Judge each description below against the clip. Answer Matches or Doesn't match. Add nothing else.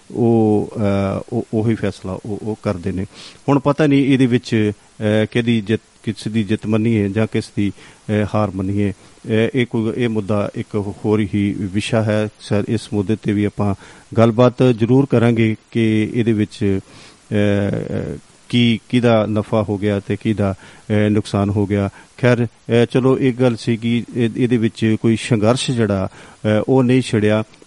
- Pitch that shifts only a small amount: Matches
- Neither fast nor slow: Matches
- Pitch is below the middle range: Matches